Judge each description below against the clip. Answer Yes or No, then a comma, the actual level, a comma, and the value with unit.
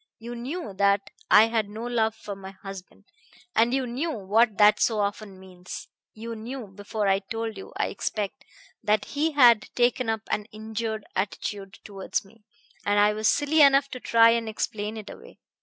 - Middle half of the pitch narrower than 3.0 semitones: Yes, narrow, 2.5 semitones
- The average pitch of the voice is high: Yes, high, 220 Hz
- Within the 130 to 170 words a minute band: No, average, 180 wpm